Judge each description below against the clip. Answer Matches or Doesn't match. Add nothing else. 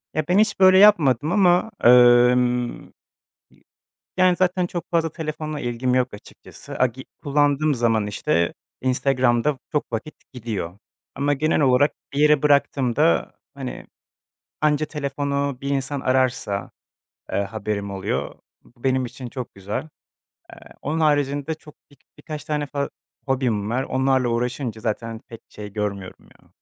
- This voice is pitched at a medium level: Doesn't match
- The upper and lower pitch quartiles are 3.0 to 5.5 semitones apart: Matches